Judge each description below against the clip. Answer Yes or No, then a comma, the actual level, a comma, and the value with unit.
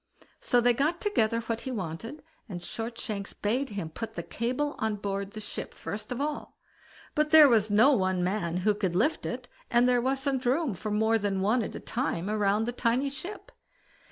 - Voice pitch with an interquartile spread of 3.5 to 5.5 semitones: Yes, average, 4.4 semitones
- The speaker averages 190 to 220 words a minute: Yes, average, 195 wpm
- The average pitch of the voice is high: Yes, high, 225 Hz